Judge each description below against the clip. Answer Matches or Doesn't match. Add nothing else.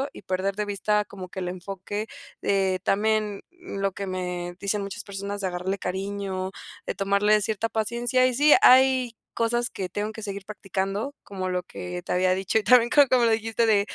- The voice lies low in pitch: Doesn't match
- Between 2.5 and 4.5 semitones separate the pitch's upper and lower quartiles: Matches